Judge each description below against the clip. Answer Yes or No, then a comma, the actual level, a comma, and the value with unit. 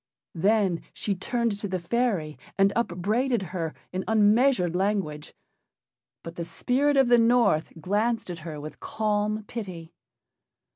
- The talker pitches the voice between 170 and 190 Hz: No, high, 205 Hz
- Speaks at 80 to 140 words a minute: Yes, slow, 135 wpm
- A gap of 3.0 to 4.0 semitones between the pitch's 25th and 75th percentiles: No, average, 5.1 semitones